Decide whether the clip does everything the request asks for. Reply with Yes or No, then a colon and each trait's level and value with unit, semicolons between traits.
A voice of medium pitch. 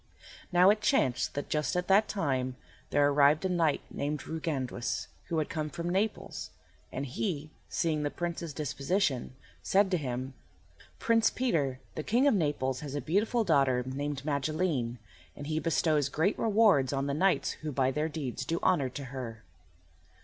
Yes: medium, 150 Hz